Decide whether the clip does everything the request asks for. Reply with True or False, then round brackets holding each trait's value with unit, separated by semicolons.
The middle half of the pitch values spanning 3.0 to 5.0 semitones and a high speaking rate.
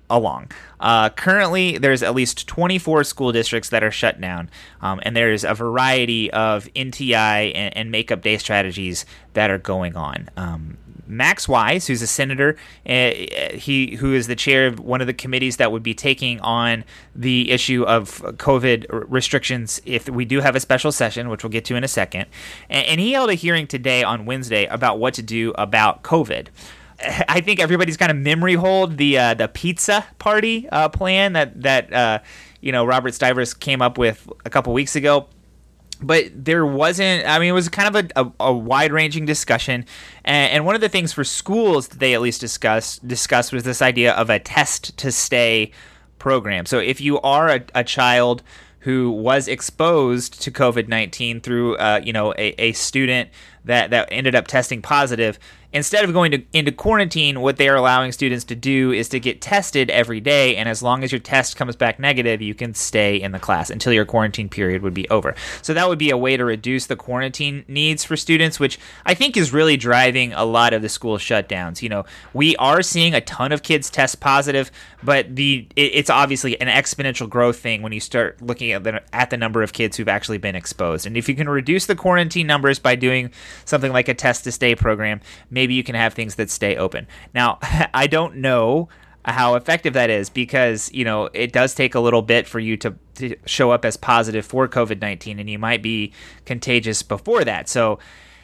True (3.9 semitones; 210 wpm)